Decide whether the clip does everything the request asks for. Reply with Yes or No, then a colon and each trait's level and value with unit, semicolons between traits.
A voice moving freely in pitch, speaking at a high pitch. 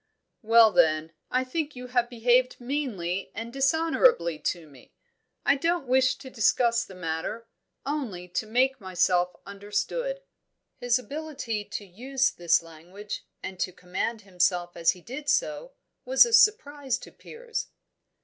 Yes: wide, 7.1 semitones; high, 235 Hz